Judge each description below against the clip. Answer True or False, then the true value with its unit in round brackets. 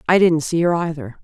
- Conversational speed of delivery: False (245 wpm)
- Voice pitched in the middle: True (160 Hz)